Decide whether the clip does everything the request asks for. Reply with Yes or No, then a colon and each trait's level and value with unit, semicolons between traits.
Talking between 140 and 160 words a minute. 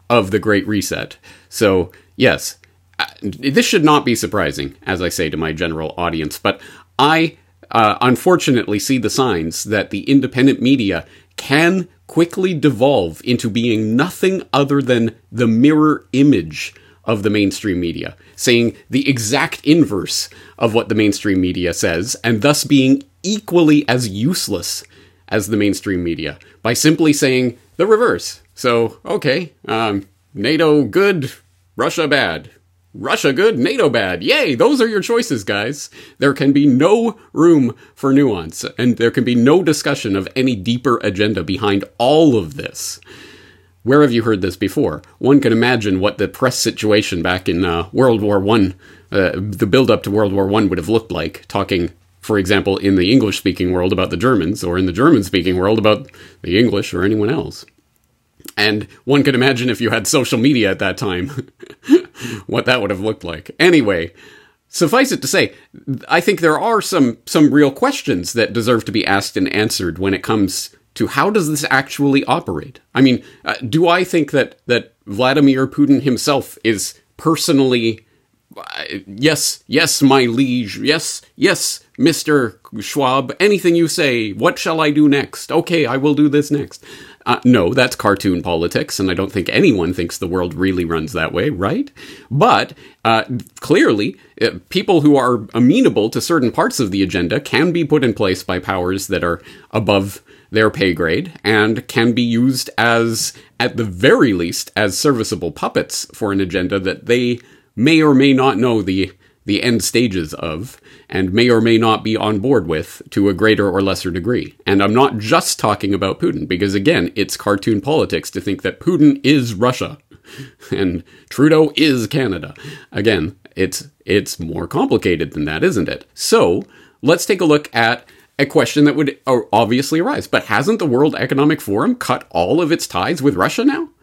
No: average, 170 wpm